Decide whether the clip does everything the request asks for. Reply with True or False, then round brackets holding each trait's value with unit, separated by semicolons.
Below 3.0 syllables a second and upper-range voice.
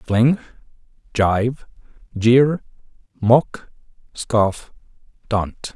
False (2.0 syllables/s; 115 Hz)